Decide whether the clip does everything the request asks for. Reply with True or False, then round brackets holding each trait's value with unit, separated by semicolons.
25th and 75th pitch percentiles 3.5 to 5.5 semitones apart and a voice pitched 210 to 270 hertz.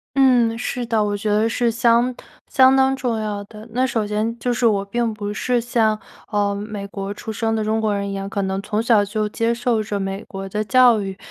False (2.5 semitones; 215 Hz)